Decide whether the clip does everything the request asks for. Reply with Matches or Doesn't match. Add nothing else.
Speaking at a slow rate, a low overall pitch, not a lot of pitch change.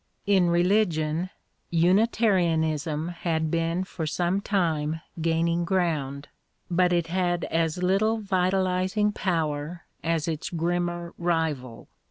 Doesn't match